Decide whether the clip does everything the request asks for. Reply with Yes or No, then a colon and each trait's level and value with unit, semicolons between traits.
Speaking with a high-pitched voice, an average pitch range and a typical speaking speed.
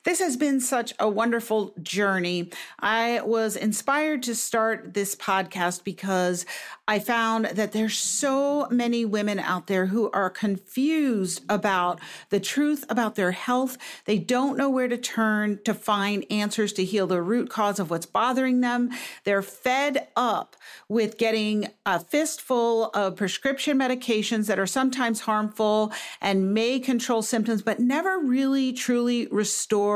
Yes: high, 220 Hz; average, 3.7 semitones; average, 150 wpm